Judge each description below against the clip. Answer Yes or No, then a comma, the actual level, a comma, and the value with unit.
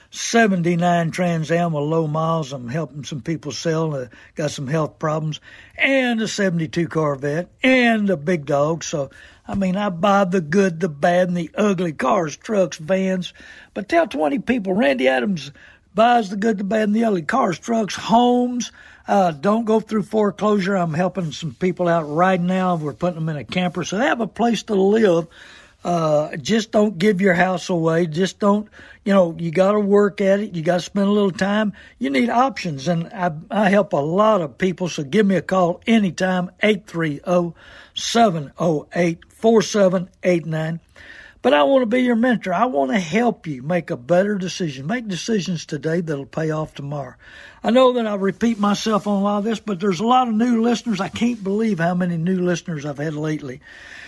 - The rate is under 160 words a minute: No, average, 190 wpm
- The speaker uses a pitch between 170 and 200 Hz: Yes, medium, 185 Hz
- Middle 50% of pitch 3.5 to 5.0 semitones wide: Yes, average, 4.3 semitones